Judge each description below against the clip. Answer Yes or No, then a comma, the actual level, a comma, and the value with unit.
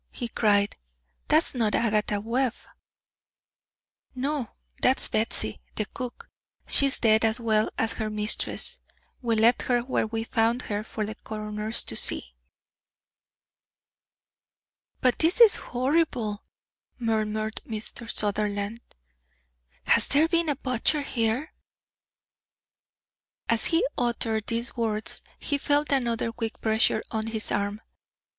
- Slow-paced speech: Yes, slow, 120 wpm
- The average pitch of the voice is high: Yes, high, 225 Hz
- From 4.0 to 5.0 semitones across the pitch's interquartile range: No, average, 2.7 semitones